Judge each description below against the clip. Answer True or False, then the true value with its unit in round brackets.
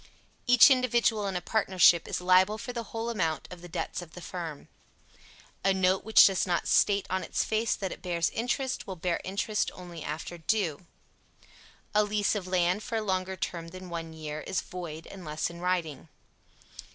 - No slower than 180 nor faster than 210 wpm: True (185 wpm)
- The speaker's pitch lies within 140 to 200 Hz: True (185 Hz)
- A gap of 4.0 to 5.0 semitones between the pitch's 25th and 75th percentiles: False (3.6 semitones)